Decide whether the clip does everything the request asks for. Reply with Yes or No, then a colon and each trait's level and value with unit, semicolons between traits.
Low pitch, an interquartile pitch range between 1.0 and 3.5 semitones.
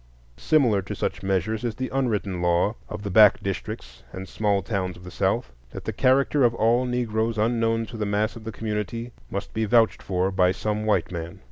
Yes: low, 105 Hz; average, 3.1 semitones